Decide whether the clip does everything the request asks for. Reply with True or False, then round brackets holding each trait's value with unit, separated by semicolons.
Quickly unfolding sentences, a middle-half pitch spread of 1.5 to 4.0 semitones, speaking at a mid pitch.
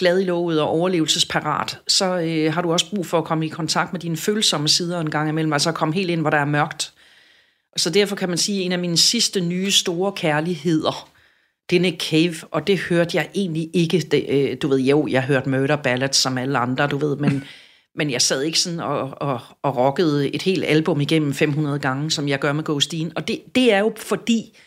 True (235 wpm; 3.3 semitones; 165 Hz)